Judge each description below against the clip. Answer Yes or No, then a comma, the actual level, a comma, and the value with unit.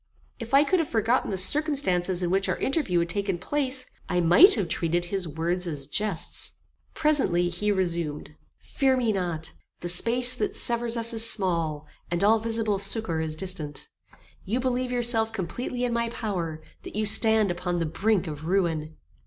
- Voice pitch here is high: Yes, high, 195 Hz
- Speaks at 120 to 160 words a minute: No, average, 175 wpm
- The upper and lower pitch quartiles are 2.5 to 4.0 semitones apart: No, average, 5.3 semitones